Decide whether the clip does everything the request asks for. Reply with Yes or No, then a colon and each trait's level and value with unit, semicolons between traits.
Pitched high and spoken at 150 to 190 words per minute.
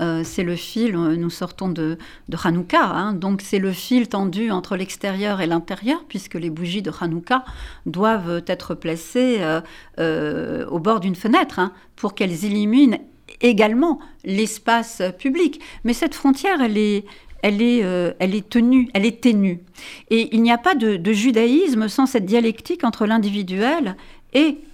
Yes: high, 210 Hz; average, 165 wpm